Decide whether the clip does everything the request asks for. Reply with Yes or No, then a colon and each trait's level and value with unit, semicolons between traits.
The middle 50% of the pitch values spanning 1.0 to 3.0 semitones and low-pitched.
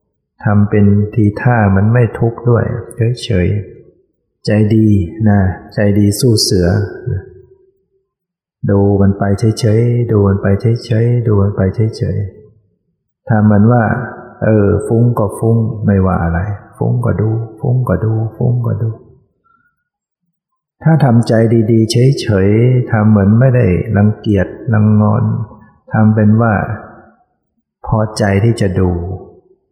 Yes: average, 2.7 semitones; low, 110 Hz